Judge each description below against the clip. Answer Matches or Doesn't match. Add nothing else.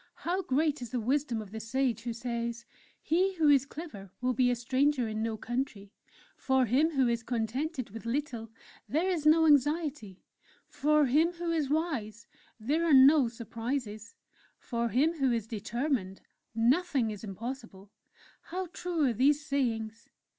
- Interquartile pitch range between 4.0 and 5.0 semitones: Matches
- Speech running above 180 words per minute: Doesn't match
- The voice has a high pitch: Matches